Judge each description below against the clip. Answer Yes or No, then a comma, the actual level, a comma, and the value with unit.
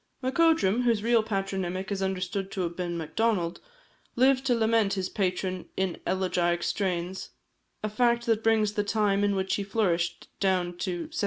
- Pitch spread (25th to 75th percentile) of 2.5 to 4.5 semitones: Yes, average, 3.4 semitones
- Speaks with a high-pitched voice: Yes, high, 195 Hz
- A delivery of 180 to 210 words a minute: No, average, 165 wpm